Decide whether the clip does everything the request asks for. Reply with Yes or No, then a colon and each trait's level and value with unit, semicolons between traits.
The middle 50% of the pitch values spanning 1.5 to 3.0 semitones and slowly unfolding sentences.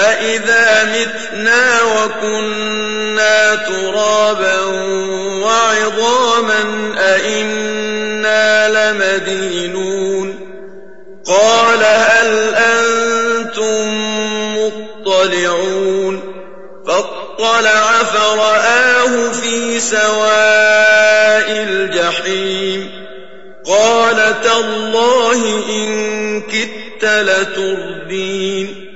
Yes: narrow, 2.5 semitones; slow, 45 wpm